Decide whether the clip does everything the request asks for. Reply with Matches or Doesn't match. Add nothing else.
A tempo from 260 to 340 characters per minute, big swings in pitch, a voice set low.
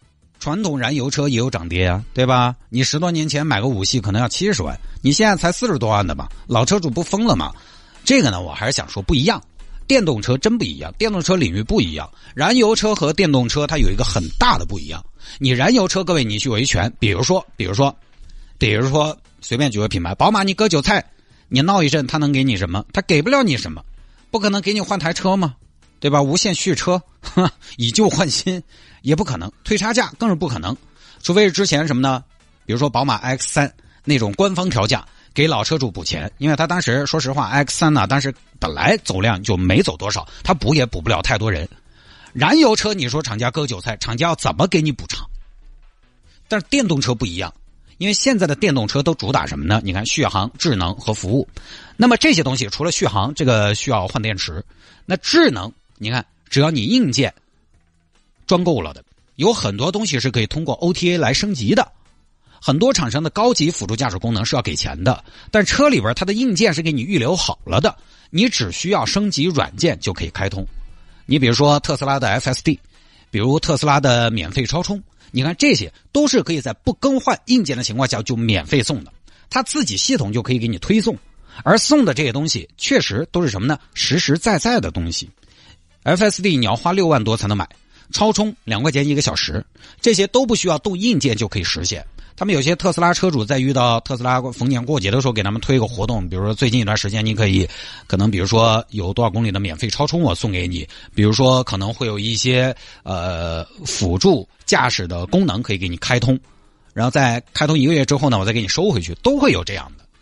Matches